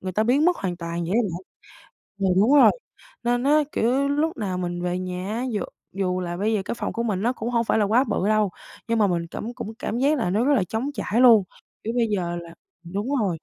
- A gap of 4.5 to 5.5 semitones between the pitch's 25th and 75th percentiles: Yes, average, 4.8 semitones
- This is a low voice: No, high, 215 Hz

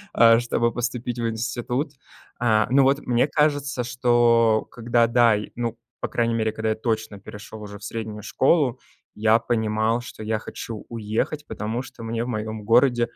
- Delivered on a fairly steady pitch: Yes, narrow, 1.8 semitones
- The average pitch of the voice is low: Yes, low, 115 Hz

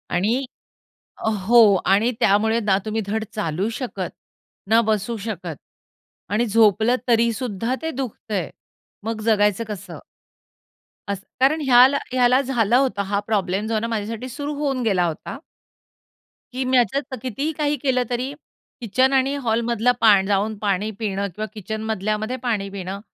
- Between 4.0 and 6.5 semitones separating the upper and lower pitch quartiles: No, average, 3.6 semitones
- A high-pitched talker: Yes, high, 225 Hz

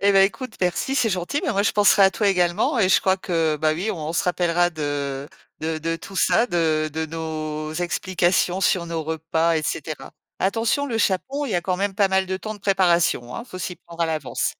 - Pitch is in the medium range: Yes, medium, 175 Hz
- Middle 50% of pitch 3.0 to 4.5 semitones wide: Yes, average, 3.4 semitones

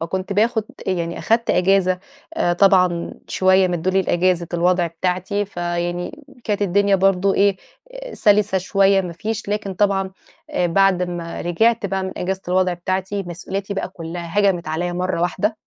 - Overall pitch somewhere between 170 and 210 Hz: Yes, medium, 185 Hz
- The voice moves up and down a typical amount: No, narrow, 2.1 semitones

